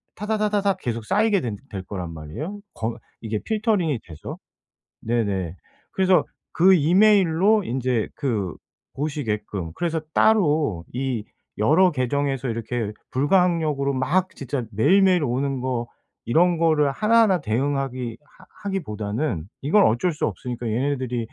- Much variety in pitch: Yes, wide, 7.6 semitones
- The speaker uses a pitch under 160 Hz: Yes, medium, 140 Hz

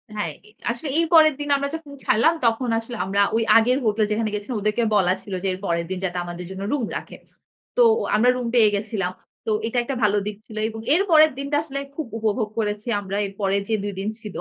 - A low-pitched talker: No, high, 220 Hz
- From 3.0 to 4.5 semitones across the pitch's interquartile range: Yes, average, 4.0 semitones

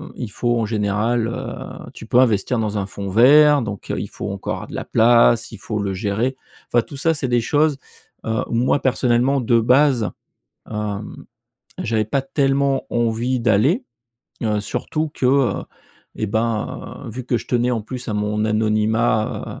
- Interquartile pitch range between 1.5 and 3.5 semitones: Yes, average, 3.2 semitones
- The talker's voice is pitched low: Yes, low, 115 Hz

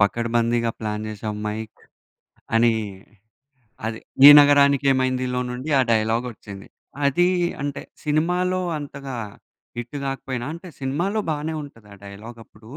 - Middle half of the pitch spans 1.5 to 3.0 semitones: No, average, 4.3 semitones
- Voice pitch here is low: Yes, low, 125 Hz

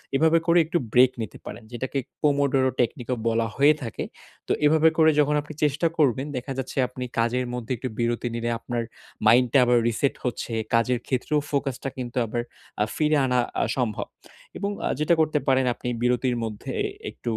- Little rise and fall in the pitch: No, average, 3.5 semitones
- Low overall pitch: Yes, low, 130 Hz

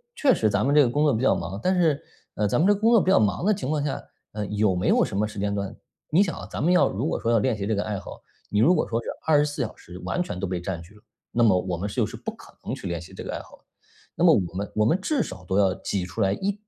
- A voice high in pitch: No, low, 110 Hz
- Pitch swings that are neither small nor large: No, wide, 7.6 semitones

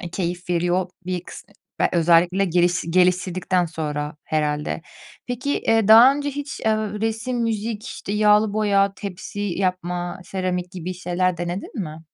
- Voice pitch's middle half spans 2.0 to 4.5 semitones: Yes, average, 3.3 semitones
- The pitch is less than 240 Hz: Yes, medium, 185 Hz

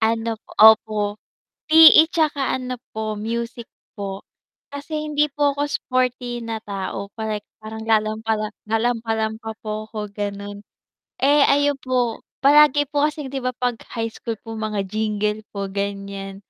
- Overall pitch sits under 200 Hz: No, high, 225 Hz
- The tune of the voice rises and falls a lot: No, average, 3.8 semitones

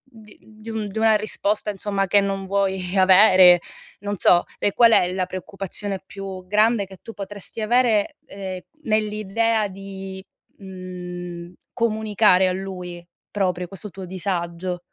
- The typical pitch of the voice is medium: No, high, 195 Hz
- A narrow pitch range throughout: Yes, narrow, 2.3 semitones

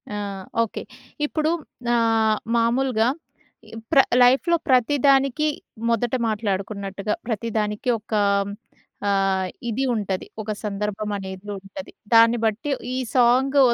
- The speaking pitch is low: No, high, 225 Hz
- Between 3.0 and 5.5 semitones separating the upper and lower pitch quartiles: Yes, average, 3.7 semitones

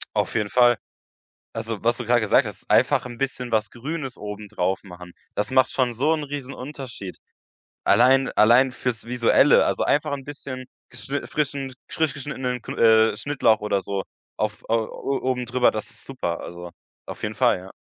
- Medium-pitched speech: No, low, 120 Hz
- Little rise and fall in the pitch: No, average, 3.8 semitones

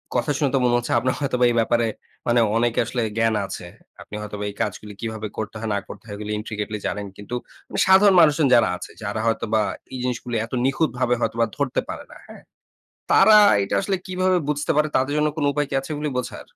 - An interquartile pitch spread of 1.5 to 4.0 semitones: No, average, 4.9 semitones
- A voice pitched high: No, low, 120 Hz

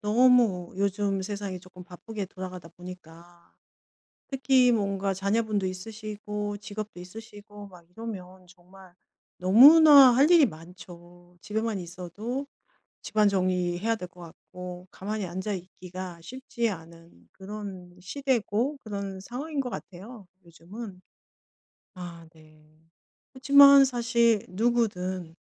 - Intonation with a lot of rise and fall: No, average, 4.1 semitones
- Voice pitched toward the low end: No, high, 195 Hz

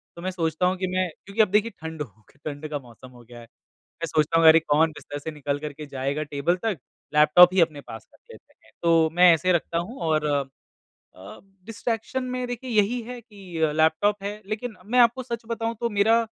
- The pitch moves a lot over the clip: Yes, wide, 6.2 semitones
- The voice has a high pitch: No, medium, 170 Hz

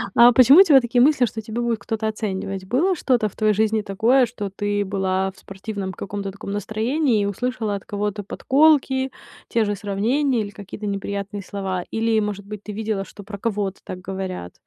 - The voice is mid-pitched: No, high, 210 Hz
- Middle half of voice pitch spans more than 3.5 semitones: No, average, 3.1 semitones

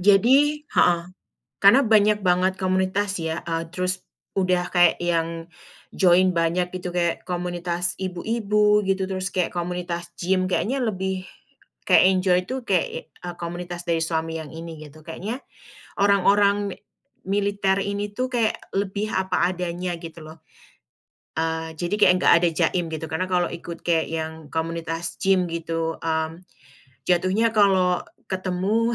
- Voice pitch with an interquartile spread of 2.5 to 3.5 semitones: Yes, average, 2.8 semitones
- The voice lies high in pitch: No, medium, 180 Hz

